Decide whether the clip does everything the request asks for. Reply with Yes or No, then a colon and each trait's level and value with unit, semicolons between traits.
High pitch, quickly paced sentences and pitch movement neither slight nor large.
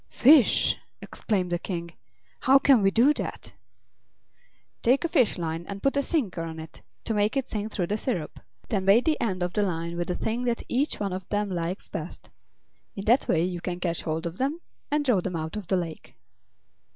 No: high, 195 Hz; fast, 210 wpm; wide, 5.9 semitones